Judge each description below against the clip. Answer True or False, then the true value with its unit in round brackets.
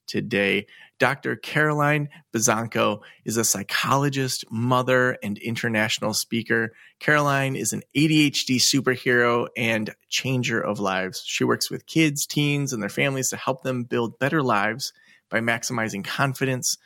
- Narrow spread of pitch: False (3.4 semitones)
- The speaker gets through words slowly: True (130 wpm)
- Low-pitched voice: True (125 Hz)